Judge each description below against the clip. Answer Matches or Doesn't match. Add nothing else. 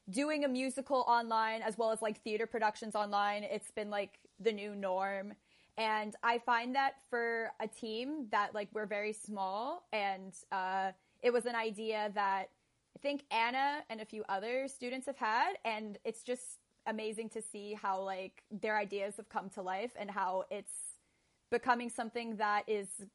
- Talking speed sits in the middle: Matches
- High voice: Matches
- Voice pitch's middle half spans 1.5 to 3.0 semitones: Matches